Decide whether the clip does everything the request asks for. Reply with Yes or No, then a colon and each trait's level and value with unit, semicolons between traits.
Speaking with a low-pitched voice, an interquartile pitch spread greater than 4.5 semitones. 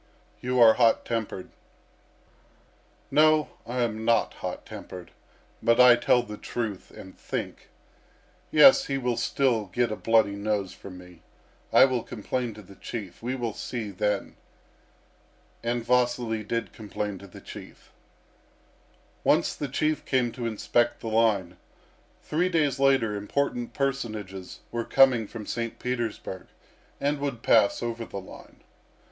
No: low, 115 Hz; average, 3.2 semitones